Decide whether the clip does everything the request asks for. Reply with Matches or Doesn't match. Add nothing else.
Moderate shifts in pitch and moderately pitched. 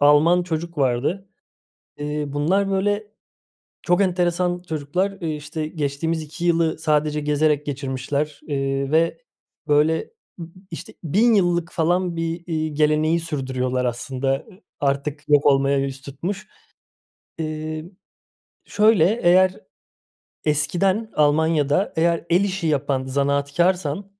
Matches